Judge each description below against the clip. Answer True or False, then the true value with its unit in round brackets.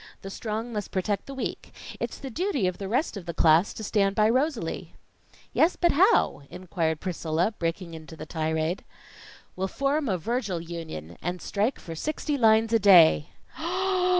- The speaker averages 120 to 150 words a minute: False (170 wpm)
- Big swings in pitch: True (6.0 semitones)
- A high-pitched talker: True (195 Hz)